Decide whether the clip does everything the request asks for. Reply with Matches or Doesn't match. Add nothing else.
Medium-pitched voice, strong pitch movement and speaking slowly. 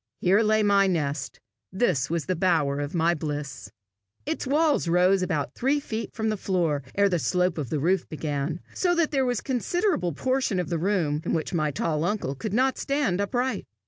Doesn't match